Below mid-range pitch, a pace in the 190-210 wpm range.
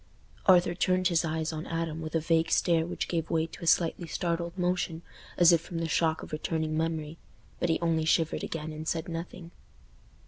No: medium, 165 Hz; average, 200 wpm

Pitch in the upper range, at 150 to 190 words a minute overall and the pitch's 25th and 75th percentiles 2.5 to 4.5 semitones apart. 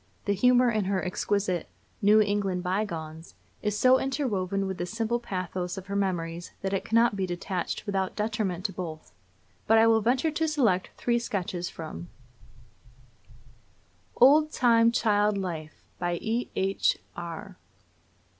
No: high, 200 Hz; average, 140 wpm; average, 3.9 semitones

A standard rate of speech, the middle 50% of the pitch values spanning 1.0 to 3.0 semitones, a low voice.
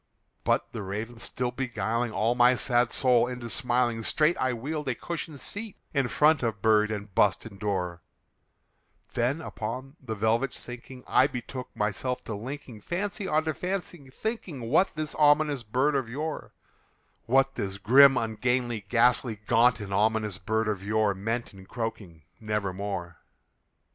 No: average, 155 wpm; average, 4.0 semitones; low, 120 Hz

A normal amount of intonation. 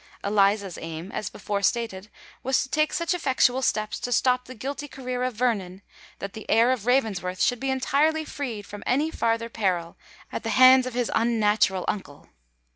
Yes: average, 4.3 semitones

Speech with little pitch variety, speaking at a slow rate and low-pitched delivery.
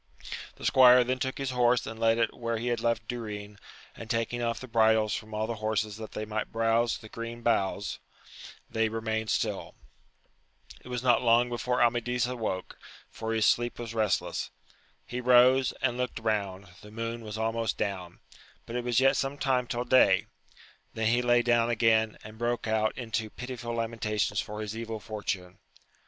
No: narrow, 1.9 semitones; average, 175 wpm; low, 115 Hz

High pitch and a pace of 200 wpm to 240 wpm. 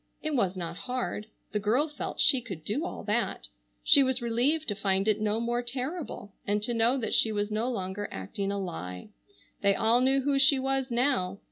Yes: high, 230 Hz; fast, 205 wpm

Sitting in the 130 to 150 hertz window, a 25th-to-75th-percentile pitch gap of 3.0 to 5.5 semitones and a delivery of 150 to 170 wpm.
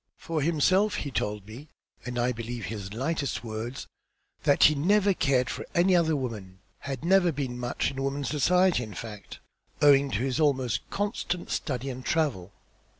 Yes: low, 135 Hz; average, 5.1 semitones; average, 165 wpm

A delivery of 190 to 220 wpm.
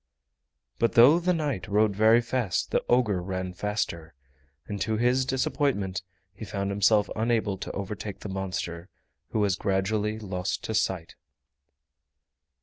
No: average, 140 wpm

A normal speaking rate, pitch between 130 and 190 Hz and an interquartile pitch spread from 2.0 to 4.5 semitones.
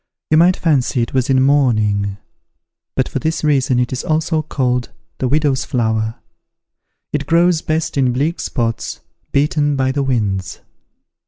Yes: average, 150 wpm; low, 135 Hz; average, 4.0 semitones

